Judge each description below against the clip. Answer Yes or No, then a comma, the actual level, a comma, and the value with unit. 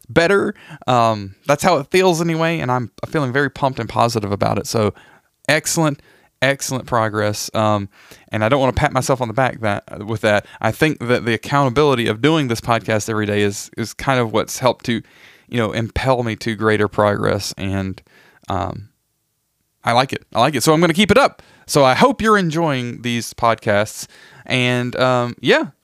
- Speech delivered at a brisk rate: No, average, 195 wpm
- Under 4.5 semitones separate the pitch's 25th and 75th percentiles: No, average, 4.8 semitones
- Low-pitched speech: Yes, low, 120 Hz